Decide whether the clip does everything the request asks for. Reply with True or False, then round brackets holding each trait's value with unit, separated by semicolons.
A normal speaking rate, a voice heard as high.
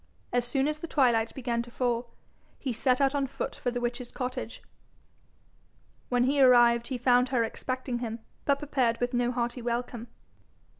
True (170 wpm; 245 Hz)